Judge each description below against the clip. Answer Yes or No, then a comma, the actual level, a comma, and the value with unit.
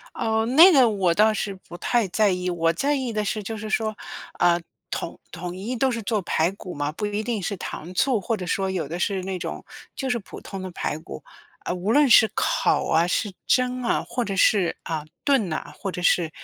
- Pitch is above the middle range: Yes, high, 200 Hz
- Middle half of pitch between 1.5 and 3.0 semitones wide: No, average, 4.3 semitones